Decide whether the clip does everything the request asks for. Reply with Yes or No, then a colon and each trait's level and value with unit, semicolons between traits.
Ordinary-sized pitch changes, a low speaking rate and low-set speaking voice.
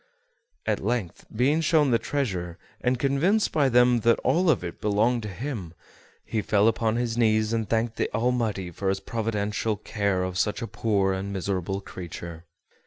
No: average, 4.0 semitones; average, 175 wpm; low, 110 Hz